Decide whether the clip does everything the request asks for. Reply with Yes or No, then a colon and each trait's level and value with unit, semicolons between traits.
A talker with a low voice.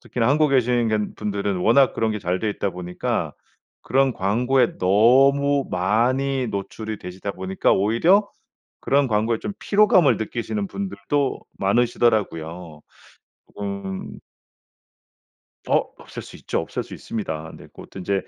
Yes: low, 110 Hz